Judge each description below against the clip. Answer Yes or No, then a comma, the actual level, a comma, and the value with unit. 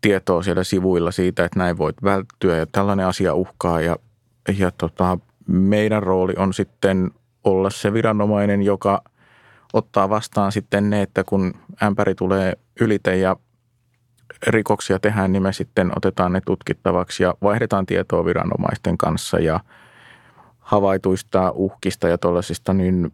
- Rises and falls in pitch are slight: Yes, narrow, 2.0 semitones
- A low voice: Yes, very low, 95 Hz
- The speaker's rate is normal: Yes, average, 135 wpm